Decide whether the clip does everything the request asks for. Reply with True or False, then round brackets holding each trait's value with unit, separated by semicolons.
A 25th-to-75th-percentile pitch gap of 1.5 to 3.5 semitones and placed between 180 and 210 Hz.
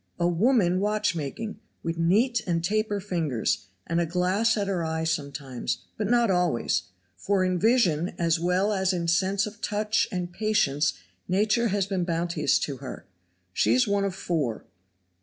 False (3.9 semitones; 185 Hz)